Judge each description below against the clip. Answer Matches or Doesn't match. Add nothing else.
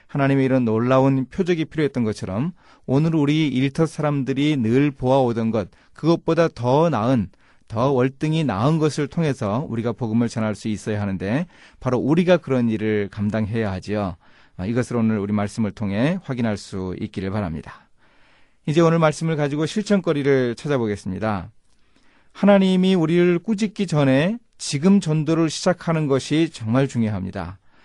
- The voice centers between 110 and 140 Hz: Matches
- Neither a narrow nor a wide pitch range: Doesn't match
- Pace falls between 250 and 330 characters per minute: Doesn't match